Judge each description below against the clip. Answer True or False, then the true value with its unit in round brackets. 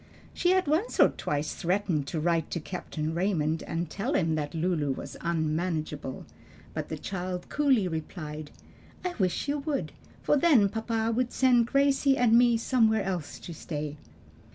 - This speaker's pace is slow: False (160 wpm)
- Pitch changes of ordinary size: False (7.5 semitones)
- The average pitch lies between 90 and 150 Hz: False (185 Hz)